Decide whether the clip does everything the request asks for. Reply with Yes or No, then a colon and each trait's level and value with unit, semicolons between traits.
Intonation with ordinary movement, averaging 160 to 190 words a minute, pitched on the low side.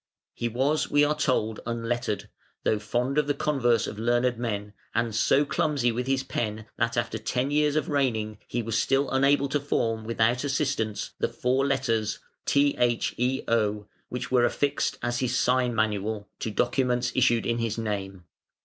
Yes: average, 3.3 semitones; average, 165 wpm; low, 120 Hz